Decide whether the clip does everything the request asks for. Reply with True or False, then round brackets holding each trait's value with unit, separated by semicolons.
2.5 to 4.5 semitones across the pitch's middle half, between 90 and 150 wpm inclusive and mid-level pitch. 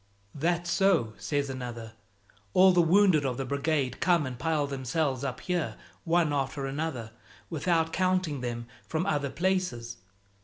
False (4.9 semitones; 145 wpm; 145 Hz)